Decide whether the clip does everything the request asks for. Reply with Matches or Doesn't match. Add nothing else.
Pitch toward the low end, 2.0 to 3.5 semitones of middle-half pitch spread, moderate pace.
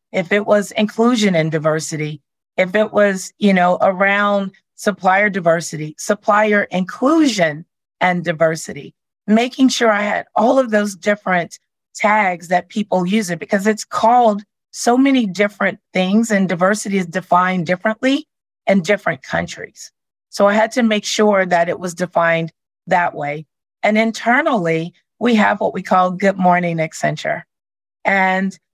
Doesn't match